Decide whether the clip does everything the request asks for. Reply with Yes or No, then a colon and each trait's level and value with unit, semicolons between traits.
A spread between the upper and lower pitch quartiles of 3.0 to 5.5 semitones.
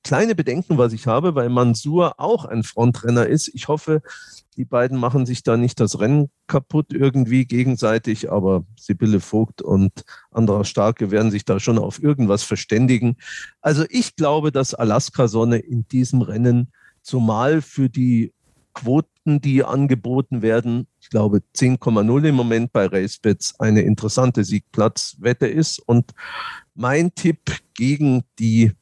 Yes: average, 3.7 semitones